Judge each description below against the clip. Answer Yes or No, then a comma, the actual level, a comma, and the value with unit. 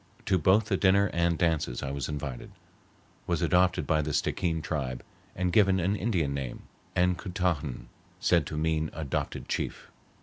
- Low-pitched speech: Yes, very low, 85 Hz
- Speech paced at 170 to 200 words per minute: No, average, 155 wpm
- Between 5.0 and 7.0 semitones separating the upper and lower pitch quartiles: No, average, 3.7 semitones